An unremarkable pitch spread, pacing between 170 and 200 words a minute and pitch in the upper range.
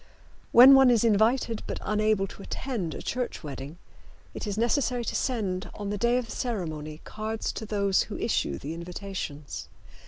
Yes: average, 4.8 semitones; average, 175 wpm; high, 210 Hz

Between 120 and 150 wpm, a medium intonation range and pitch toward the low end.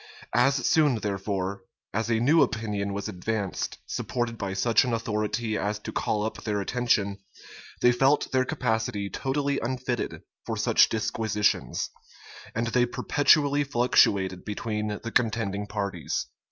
Yes: slow, 135 wpm; average, 3.3 semitones; low, 110 Hz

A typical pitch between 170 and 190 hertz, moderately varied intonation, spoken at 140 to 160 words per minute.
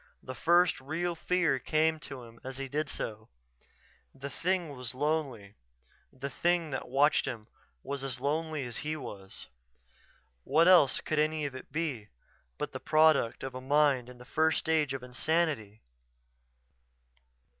No: medium, 140 Hz; average, 3.8 semitones; average, 155 wpm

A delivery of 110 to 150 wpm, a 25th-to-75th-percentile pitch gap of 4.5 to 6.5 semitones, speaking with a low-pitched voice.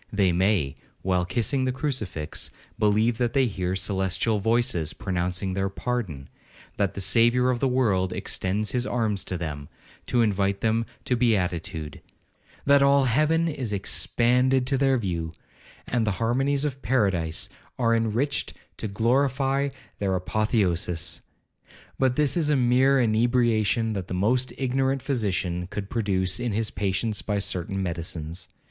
Yes: average, 145 wpm; average, 5.1 semitones; low, 110 Hz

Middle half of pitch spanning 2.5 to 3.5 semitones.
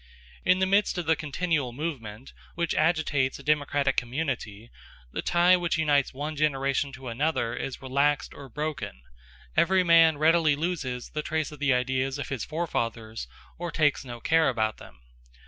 No: average, 3.9 semitones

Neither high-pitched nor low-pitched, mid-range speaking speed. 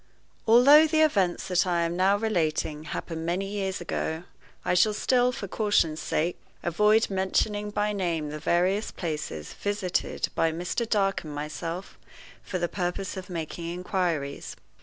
Yes: medium, 180 Hz; average, 150 wpm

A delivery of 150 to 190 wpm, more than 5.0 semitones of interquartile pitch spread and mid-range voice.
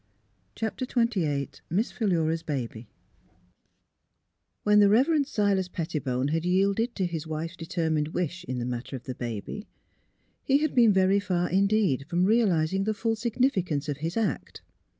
Yes: average, 155 wpm; wide, 5.5 semitones; medium, 180 Hz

